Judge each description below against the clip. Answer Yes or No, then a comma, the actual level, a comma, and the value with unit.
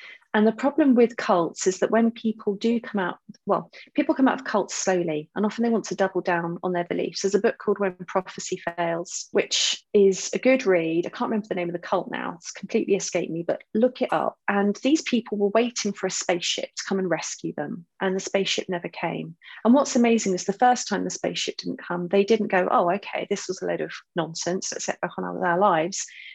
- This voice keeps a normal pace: No, fast, 240 wpm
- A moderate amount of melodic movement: Yes, average, 3.9 semitones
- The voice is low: No, high, 200 Hz